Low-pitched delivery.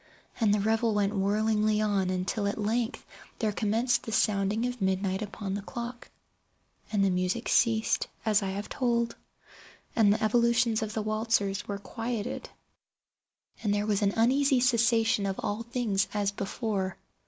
No: high, 215 Hz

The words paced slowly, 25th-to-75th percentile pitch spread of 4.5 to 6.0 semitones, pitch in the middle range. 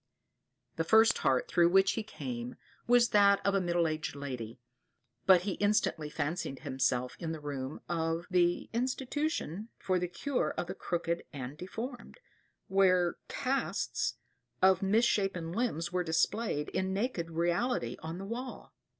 No: average, 150 wpm; average, 5.2 semitones; medium, 180 Hz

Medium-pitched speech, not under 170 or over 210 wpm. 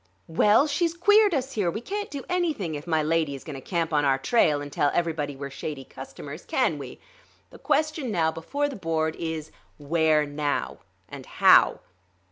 Yes: medium, 165 Hz; average, 185 wpm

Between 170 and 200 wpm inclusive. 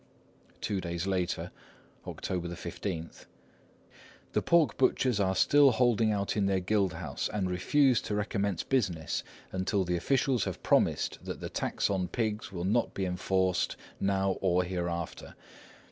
No: average, 145 wpm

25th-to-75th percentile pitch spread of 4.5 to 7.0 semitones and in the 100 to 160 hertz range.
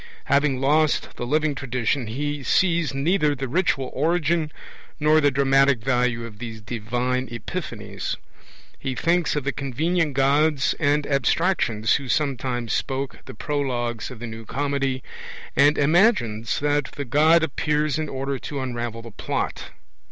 No: average, 3.4 semitones; medium, 140 Hz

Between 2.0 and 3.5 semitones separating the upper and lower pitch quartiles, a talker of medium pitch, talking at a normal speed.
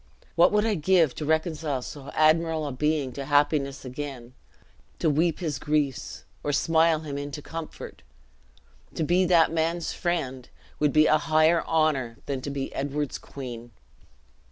Yes: average, 2.8 semitones; medium, 150 Hz; average, 155 wpm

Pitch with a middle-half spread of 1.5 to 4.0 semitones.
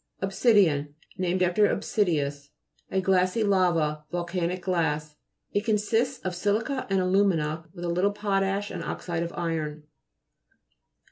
Yes: average, 3.6 semitones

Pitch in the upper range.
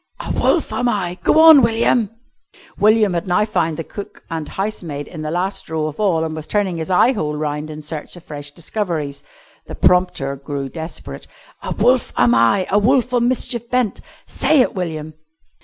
No: medium, 175 Hz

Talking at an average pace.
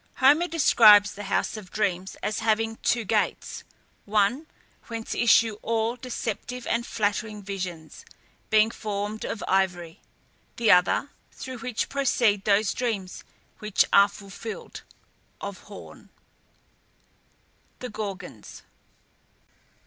No: slow, 110 wpm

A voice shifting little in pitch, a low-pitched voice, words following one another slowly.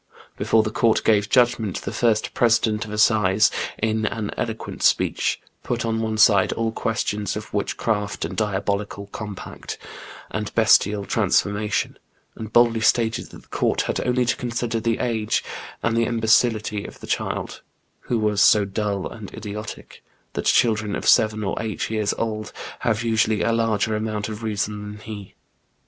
No: narrow, 1.5 semitones; low, 110 Hz; average, 160 wpm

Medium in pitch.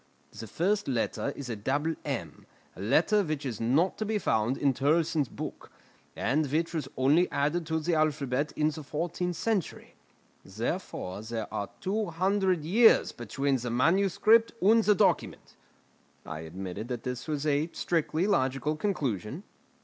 Yes: medium, 150 Hz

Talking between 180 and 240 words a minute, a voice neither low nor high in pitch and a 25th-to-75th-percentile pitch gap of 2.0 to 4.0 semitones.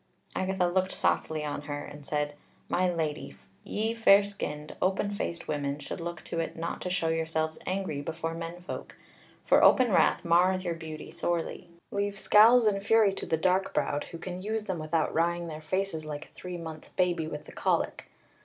Yes: average, 190 wpm; medium, 170 Hz; average, 3.3 semitones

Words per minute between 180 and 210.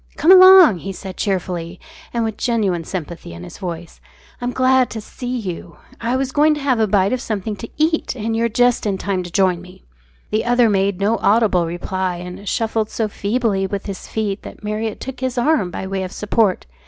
Yes: fast, 205 wpm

